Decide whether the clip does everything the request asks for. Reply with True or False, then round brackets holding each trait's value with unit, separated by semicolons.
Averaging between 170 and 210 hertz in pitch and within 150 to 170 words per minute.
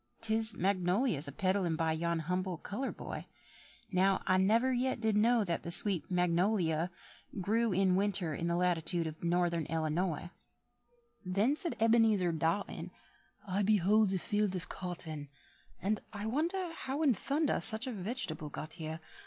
True (185 Hz; 160 wpm)